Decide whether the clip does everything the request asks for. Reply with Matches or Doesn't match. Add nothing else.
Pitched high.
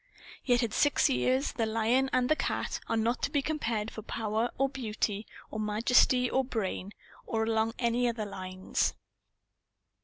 Matches